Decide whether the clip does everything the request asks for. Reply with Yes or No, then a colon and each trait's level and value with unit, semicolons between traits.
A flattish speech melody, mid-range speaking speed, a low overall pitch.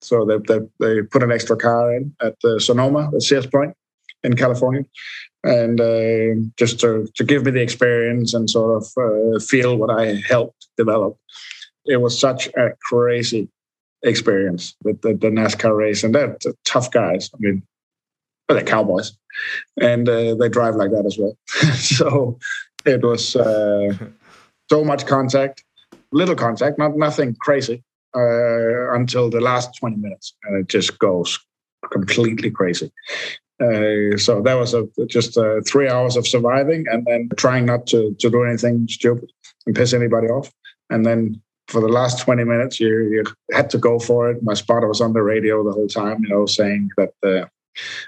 Yes: narrow, 2.1 semitones; average, 170 wpm; low, 120 Hz